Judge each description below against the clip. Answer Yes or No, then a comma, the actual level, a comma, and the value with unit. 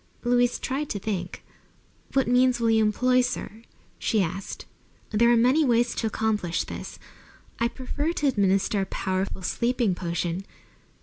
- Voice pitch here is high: Yes, high, 225 Hz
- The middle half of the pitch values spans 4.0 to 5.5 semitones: Yes, average, 4.3 semitones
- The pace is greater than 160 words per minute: No, average, 145 wpm